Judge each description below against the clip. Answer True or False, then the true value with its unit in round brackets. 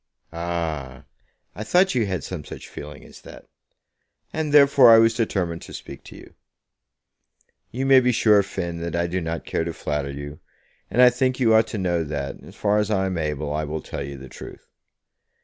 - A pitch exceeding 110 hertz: False (90 Hz)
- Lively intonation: True (6.8 semitones)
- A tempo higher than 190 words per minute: True (200 wpm)